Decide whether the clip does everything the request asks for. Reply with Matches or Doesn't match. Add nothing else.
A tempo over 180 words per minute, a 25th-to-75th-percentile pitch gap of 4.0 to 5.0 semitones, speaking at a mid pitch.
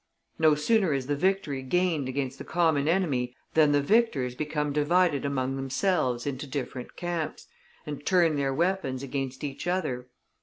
Doesn't match